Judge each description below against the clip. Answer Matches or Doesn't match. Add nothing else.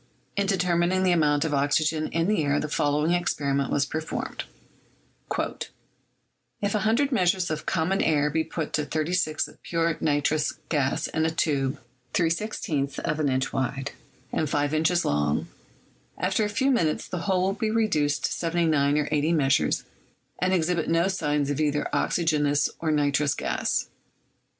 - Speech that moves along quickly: Doesn't match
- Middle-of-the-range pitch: Matches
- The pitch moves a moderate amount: Matches